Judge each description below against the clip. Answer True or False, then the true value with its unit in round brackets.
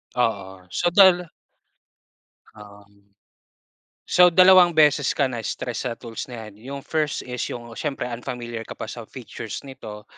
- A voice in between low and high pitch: False (125 Hz)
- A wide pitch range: True (5.7 semitones)